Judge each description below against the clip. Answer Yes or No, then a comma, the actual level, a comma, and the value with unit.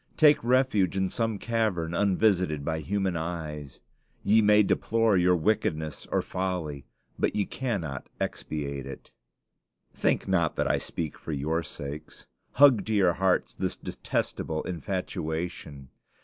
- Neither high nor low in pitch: No, very low, 90 Hz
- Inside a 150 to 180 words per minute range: No, slow, 135 wpm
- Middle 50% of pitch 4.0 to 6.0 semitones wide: Yes, average, 5.2 semitones